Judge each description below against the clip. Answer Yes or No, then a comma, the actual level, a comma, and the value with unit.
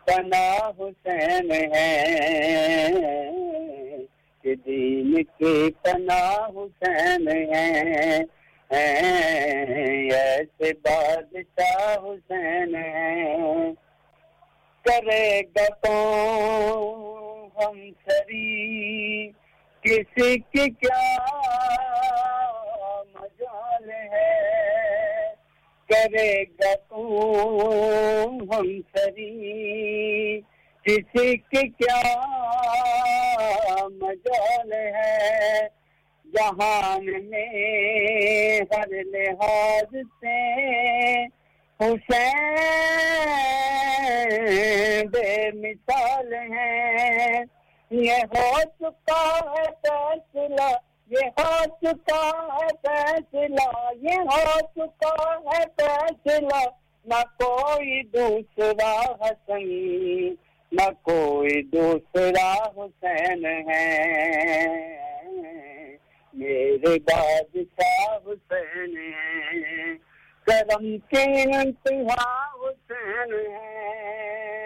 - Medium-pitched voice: No, high, 220 Hz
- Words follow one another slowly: Yes, slow, 55 wpm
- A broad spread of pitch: Yes, wide, 7.7 semitones